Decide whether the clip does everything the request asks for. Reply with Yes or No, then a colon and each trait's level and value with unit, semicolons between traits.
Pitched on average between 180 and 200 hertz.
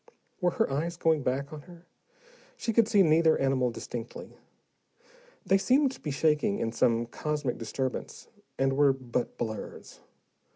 No: medium, 145 Hz